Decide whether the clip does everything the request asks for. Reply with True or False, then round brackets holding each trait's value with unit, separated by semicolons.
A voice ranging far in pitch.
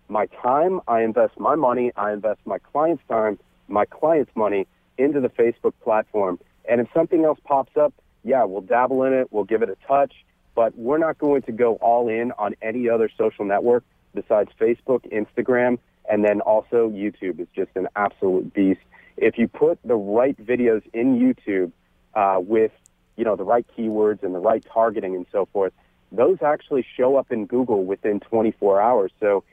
False (3.3 semitones)